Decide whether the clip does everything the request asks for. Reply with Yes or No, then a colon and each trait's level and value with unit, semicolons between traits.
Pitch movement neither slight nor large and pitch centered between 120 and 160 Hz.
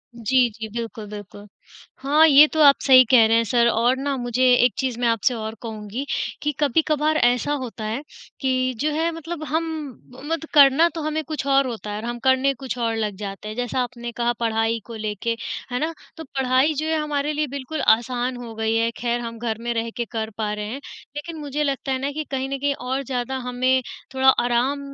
No: average, 3.5 semitones; very high, 255 Hz